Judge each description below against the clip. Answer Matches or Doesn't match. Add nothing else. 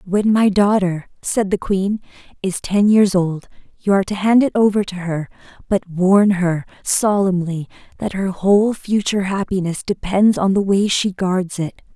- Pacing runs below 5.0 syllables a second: Matches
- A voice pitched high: Matches